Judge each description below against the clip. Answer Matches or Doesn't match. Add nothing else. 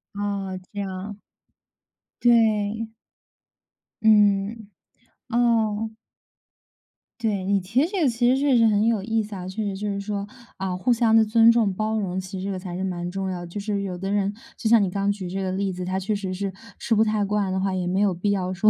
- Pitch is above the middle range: Matches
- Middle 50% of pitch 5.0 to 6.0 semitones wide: Doesn't match